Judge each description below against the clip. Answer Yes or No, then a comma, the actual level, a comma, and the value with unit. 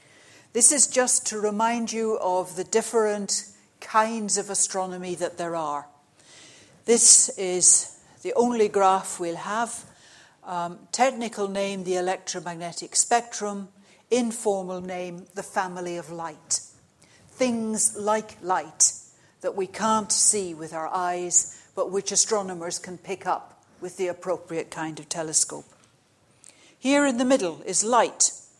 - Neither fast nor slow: No, slow, 130 wpm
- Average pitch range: Yes, average, 3.8 semitones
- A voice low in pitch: No, high, 195 Hz